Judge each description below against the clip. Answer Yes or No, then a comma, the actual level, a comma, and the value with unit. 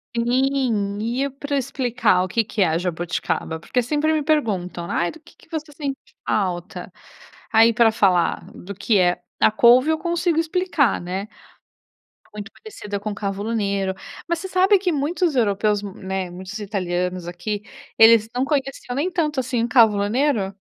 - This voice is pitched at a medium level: No, high, 225 Hz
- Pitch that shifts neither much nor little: No, wide, 6.3 semitones